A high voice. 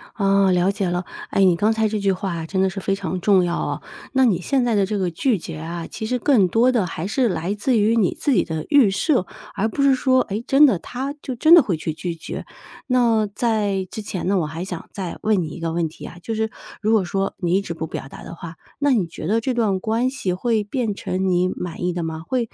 Yes: high, 200 Hz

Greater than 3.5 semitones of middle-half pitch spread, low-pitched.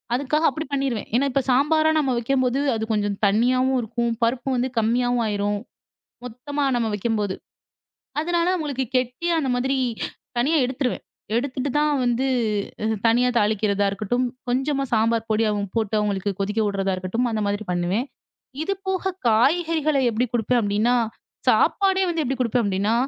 No: average, 4.3 semitones; high, 245 Hz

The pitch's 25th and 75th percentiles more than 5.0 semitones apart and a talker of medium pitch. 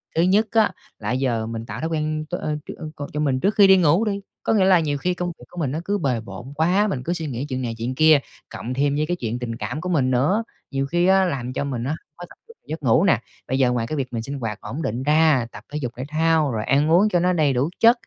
Yes: wide, 5.6 semitones; medium, 150 Hz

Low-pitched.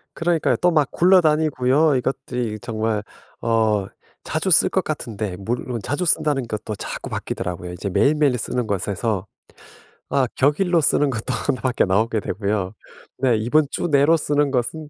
Yes: low, 125 Hz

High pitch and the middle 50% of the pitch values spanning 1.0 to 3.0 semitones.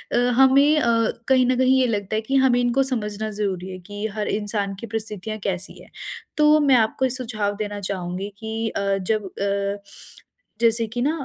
No: high, 220 Hz; average, 3.5 semitones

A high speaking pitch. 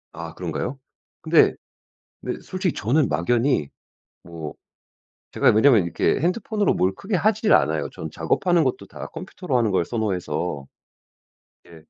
No: low, 120 Hz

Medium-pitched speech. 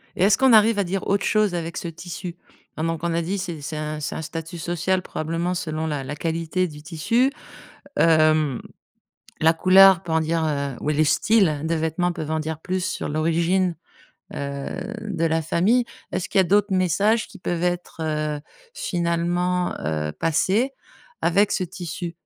Yes: medium, 170 Hz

